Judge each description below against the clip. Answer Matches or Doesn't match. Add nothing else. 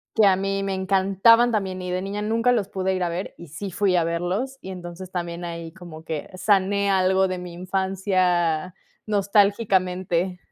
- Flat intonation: Matches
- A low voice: Doesn't match